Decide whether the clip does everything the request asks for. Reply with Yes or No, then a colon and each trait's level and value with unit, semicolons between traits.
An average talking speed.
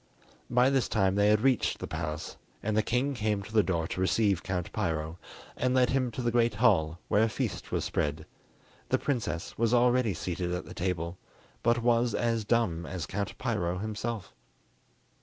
Yes: average, 185 wpm